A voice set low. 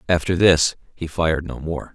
Yes: very low, 80 Hz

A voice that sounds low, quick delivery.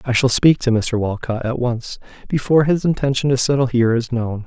Yes: low, 125 Hz; fast, 215 wpm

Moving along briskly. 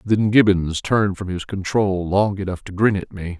Yes: fast, 210 wpm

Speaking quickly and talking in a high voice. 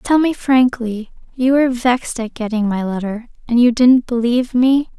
No: average, 180 wpm; high, 245 Hz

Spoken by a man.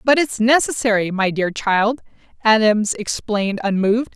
No: female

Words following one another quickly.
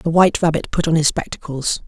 Yes: fast, 225 wpm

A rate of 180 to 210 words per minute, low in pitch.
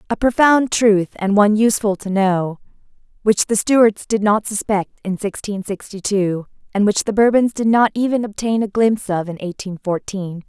No: average, 185 wpm; high, 205 Hz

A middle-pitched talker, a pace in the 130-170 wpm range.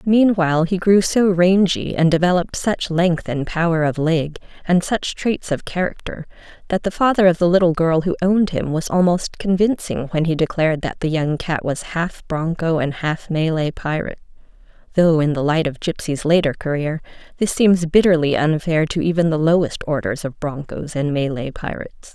No: medium, 165 Hz; average, 180 wpm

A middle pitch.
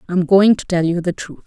Yes: medium, 180 Hz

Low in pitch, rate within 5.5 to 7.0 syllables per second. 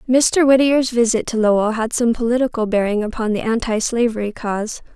No: high, 230 Hz; 5.6 syllables/s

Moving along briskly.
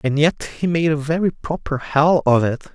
Yes: fast, 220 wpm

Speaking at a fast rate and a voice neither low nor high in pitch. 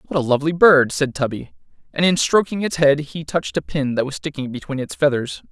Yes: fast, 230 wpm; medium, 145 Hz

